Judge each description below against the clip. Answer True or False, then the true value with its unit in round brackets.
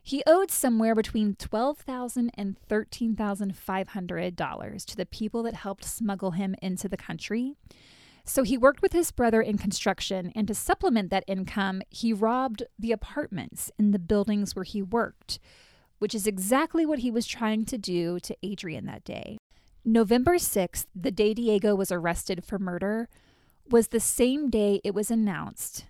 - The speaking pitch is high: True (215 Hz)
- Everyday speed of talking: True (170 wpm)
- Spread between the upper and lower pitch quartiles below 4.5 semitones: True (3.3 semitones)